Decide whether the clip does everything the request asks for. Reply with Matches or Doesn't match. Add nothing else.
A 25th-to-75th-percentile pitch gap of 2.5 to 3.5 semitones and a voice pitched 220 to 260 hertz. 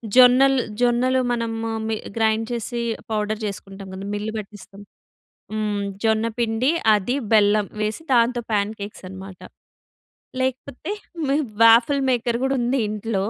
Matches